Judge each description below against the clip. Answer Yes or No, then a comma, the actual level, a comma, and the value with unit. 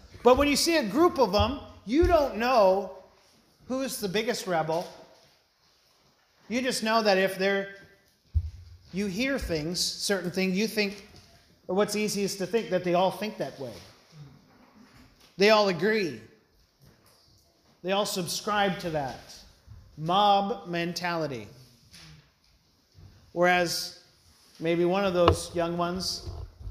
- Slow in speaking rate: Yes, slow, 125 wpm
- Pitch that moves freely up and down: No, average, 4.9 semitones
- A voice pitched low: No, medium, 185 Hz